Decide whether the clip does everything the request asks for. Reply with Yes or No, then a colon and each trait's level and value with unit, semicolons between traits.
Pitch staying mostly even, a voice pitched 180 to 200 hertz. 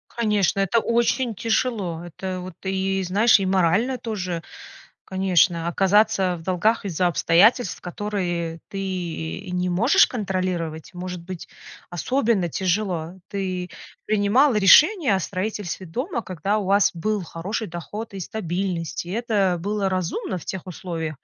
No: average, 3.2 semitones; high, 190 Hz